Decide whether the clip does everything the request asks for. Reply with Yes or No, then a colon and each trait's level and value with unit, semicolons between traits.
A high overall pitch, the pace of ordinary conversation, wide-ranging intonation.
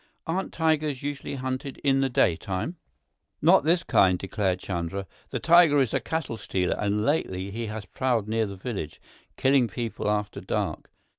No: low, 115 Hz; average, 160 wpm; wide, 6.2 semitones